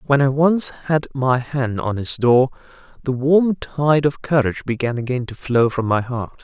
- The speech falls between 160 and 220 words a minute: Yes, average, 195 wpm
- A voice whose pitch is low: Yes, low, 130 Hz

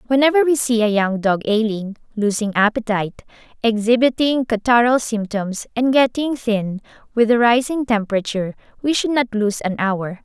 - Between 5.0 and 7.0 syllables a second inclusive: Yes, 5.1 syllables/s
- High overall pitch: Yes, high, 225 Hz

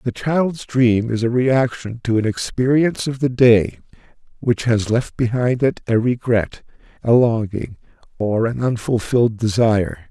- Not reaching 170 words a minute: Yes, average, 150 wpm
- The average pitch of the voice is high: No, low, 120 Hz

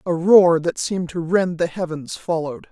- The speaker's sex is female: Yes, female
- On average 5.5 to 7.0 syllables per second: No, 5.0 syllables/s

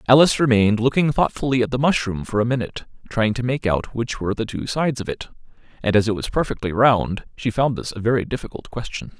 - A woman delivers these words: No, male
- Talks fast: Yes, fast, 220 wpm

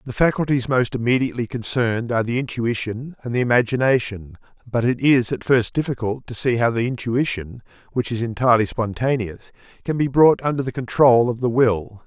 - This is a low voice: Yes, low, 120 Hz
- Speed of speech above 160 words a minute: Yes, average, 175 wpm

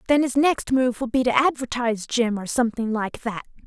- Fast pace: Yes, fast, 215 wpm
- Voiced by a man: No, female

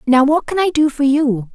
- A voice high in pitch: Yes, very high, 280 Hz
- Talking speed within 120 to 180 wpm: No, fast, 270 wpm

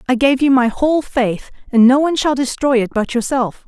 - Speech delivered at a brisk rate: Yes, fast, 230 wpm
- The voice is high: Yes, very high, 255 Hz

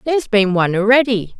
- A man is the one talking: No, female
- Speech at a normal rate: Yes, average, 170 wpm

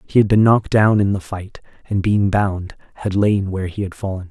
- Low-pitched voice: Yes, low, 100 Hz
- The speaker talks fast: Yes, fast, 235 wpm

